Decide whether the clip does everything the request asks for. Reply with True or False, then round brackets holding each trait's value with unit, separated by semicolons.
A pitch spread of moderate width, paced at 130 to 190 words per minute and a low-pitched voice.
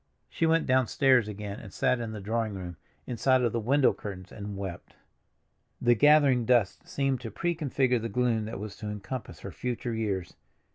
True (3.9 semitones; 180 wpm; 115 Hz)